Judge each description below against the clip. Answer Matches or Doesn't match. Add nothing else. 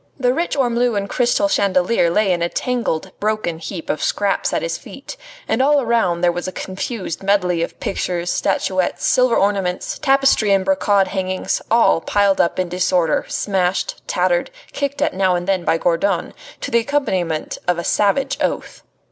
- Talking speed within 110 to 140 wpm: Doesn't match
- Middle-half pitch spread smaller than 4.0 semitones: Doesn't match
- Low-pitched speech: Doesn't match